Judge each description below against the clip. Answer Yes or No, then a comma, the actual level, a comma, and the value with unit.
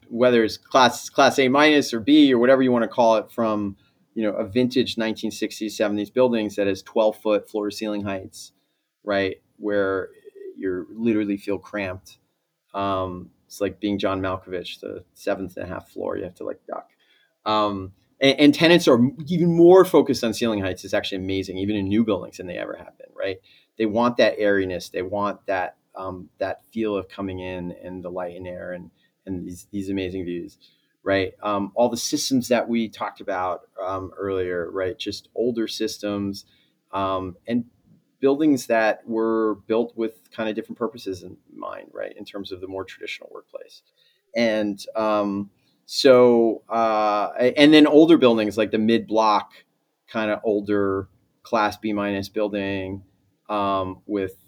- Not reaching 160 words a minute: No, average, 175 wpm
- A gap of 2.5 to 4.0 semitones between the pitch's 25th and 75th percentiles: Yes, average, 3.7 semitones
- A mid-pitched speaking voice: No, low, 105 Hz